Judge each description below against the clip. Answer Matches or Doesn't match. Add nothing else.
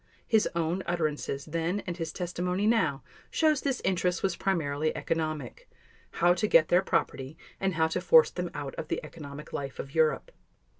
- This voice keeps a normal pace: Matches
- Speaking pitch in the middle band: Matches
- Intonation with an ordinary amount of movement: Matches